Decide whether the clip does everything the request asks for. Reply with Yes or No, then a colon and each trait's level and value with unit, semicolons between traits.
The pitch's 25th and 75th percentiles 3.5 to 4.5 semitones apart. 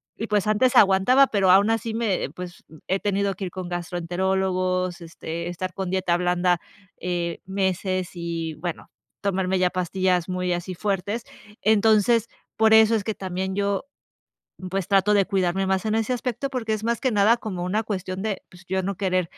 No: narrow, 2.6 semitones